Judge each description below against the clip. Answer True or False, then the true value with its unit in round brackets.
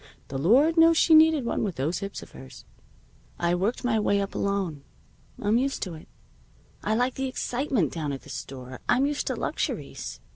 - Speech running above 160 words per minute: True (190 wpm)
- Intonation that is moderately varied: False (8.4 semitones)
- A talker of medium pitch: False (205 Hz)